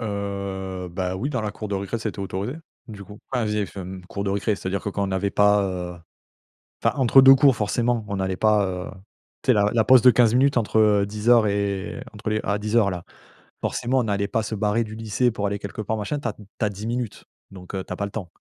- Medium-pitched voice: No, low, 105 Hz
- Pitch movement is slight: Yes, narrow, 2.3 semitones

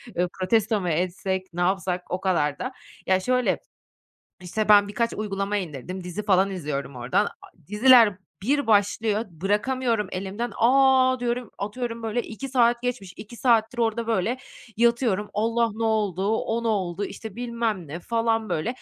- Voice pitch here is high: Yes, high, 210 Hz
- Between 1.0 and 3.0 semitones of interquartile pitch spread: No, average, 3.9 semitones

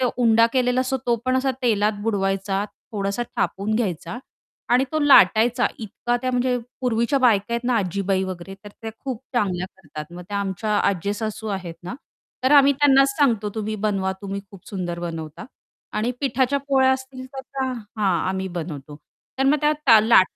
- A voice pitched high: Yes, high, 220 Hz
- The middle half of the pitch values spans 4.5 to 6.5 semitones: Yes, average, 4.9 semitones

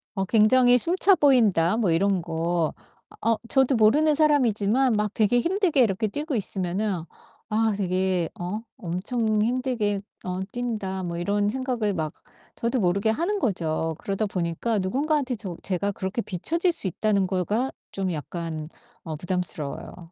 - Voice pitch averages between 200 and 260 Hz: Yes, high, 210 Hz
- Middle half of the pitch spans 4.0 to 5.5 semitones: Yes, average, 5.2 semitones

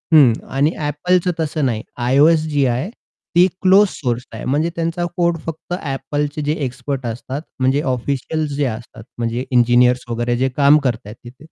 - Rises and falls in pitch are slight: No, average, 4.2 semitones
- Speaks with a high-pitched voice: No, medium, 140 Hz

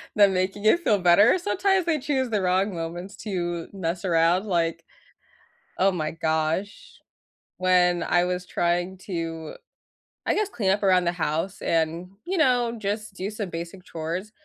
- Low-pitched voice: No, medium, 185 Hz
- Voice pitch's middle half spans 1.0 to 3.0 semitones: No, average, 3.5 semitones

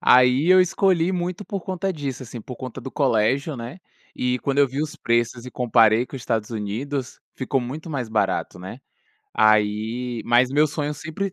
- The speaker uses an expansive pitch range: No, average, 4.3 semitones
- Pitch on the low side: Yes, low, 130 Hz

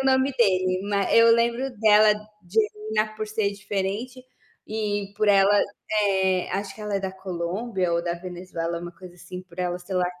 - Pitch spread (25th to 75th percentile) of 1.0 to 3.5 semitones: Yes, average, 2.9 semitones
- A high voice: Yes, high, 195 Hz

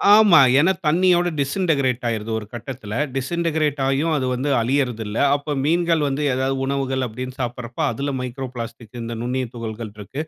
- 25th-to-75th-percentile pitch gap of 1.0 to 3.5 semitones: No, average, 3.9 semitones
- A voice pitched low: Yes, low, 130 Hz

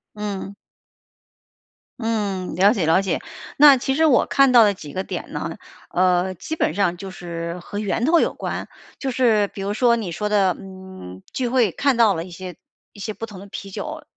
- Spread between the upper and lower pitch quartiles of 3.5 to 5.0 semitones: Yes, average, 4.2 semitones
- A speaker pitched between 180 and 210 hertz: Yes, high, 200 Hz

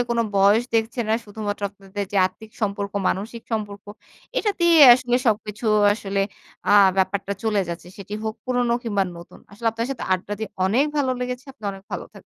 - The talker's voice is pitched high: Yes, high, 210 Hz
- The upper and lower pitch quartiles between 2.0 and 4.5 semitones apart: Yes, average, 2.9 semitones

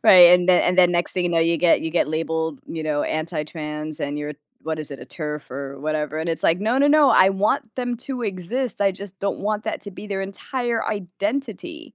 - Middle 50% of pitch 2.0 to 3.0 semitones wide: No, average, 5.1 semitones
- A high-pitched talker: No, medium, 180 Hz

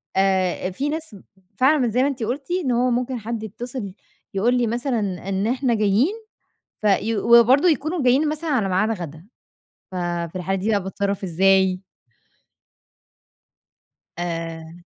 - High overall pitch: Yes, high, 225 Hz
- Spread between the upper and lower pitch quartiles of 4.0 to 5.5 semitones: Yes, average, 5.0 semitones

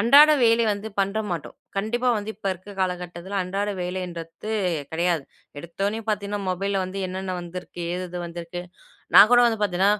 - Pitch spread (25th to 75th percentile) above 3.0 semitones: No, average, 2.7 semitones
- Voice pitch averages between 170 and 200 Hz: Yes, high, 190 Hz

